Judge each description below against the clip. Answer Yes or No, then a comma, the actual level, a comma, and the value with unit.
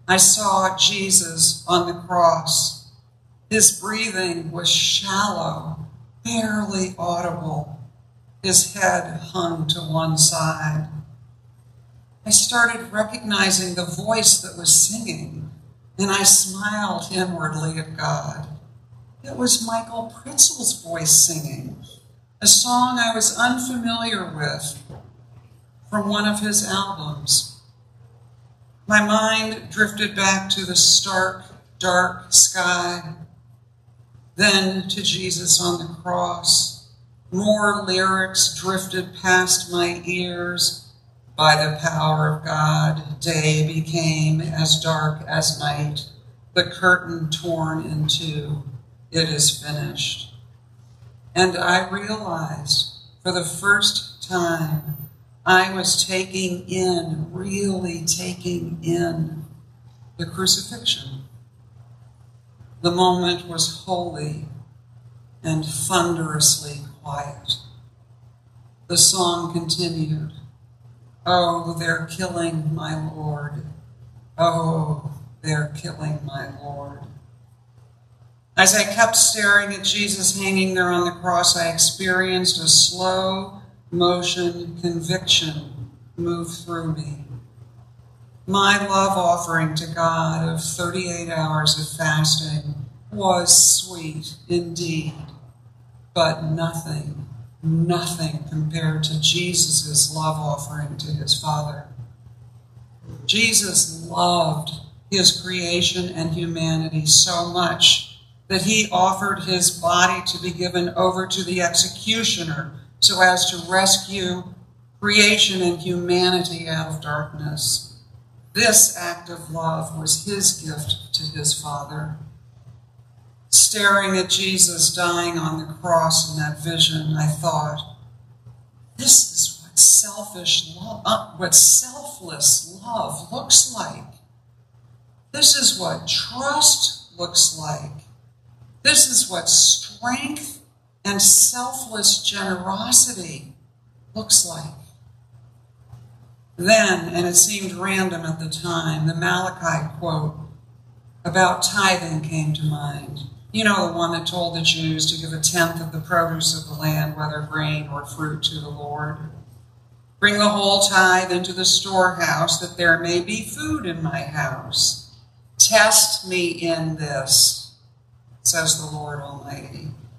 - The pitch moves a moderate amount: Yes, average, 4.8 semitones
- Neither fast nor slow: No, slow, 110 wpm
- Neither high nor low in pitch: Yes, medium, 160 Hz